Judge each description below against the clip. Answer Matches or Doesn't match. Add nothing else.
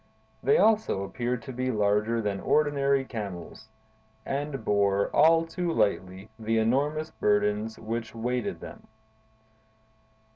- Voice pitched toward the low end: Matches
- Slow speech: Matches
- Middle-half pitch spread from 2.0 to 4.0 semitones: Doesn't match